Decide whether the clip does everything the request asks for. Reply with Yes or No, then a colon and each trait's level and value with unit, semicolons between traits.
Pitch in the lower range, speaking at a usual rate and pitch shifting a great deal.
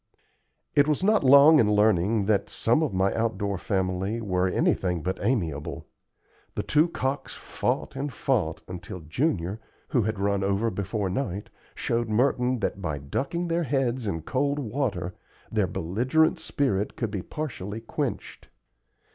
Yes: low, 110 Hz; average, 145 wpm; wide, 6.1 semitones